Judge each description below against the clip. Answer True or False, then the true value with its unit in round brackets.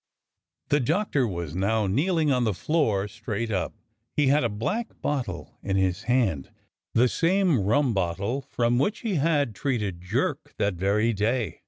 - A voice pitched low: True (115 Hz)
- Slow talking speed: False (160 wpm)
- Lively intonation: True (6.4 semitones)